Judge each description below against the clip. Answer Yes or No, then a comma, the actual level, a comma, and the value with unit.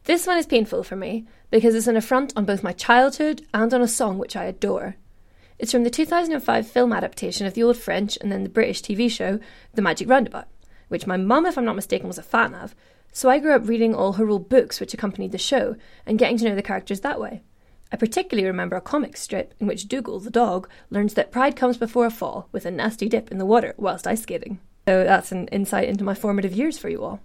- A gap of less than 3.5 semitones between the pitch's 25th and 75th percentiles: No, average, 3.8 semitones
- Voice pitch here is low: No, high, 230 Hz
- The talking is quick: Yes, fast, 245 wpm